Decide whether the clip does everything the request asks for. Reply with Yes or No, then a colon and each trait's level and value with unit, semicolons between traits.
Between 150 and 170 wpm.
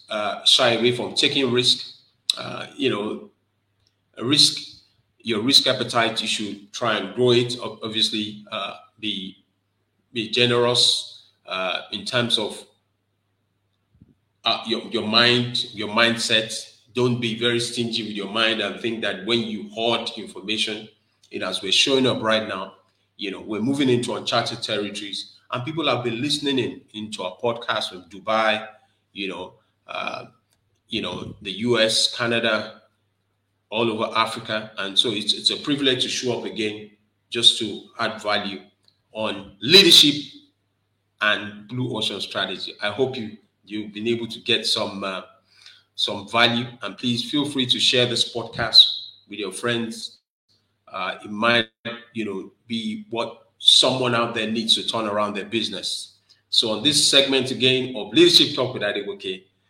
Yes: average, 155 wpm